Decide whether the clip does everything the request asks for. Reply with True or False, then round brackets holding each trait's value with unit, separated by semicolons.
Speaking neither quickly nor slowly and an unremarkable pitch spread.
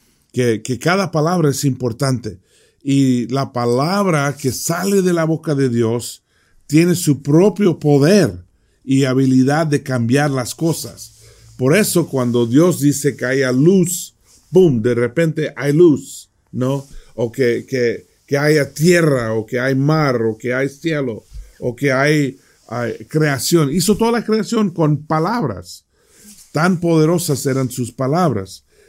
True (145 wpm; 5.0 semitones)